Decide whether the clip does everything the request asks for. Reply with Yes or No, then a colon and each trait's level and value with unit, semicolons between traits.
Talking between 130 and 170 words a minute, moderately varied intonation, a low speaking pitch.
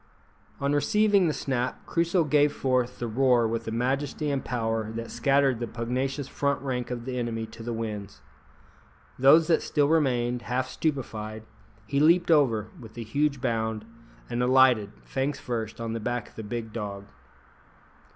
Yes: average, 165 wpm; average, 3.7 semitones; low, 125 Hz